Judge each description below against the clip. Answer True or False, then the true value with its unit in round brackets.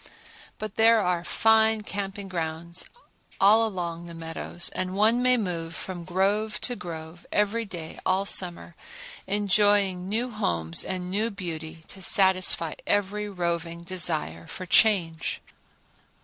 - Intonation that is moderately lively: True (3.5 semitones)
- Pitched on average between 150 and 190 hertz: True (185 Hz)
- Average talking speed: False (130 wpm)